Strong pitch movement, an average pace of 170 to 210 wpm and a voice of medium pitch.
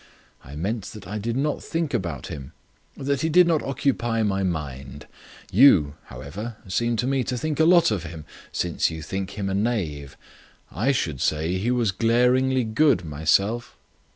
No: wide, 7.5 semitones; average, 175 wpm; low, 105 Hz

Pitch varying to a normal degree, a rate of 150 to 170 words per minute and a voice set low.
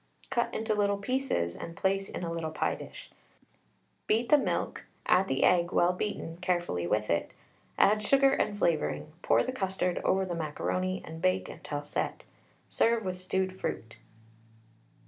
No: average, 4.2 semitones; average, 160 wpm; medium, 185 Hz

